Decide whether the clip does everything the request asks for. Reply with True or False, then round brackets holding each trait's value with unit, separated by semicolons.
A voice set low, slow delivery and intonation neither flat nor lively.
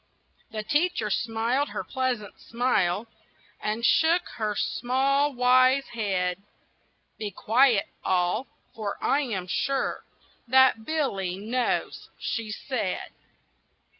False (235 Hz; 105 wpm; 4.0 semitones)